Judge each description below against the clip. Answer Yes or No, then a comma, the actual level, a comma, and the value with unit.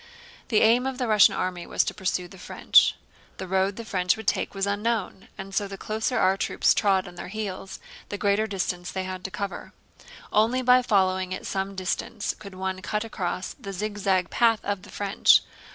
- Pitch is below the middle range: No, high, 195 Hz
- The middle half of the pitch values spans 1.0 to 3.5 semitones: Yes, narrow, 2.4 semitones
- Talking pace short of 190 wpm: No, average, 200 wpm